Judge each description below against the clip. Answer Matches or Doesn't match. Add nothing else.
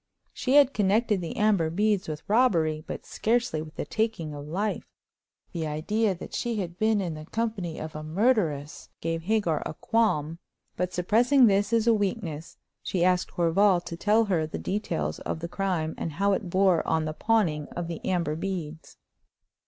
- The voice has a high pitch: Doesn't match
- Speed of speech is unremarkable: Matches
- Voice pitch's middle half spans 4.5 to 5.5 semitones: Matches